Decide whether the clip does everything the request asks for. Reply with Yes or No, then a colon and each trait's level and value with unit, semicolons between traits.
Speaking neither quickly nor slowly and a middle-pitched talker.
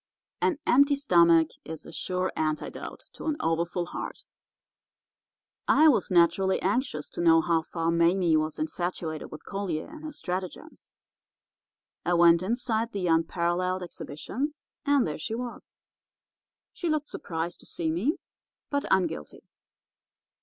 No: slow, 130 wpm; medium, 180 Hz